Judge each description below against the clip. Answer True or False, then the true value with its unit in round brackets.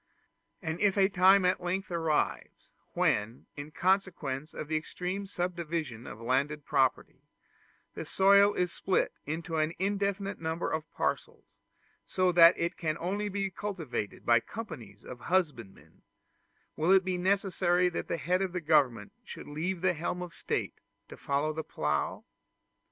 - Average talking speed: True (150 wpm)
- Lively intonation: False (4.0 semitones)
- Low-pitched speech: False (170 Hz)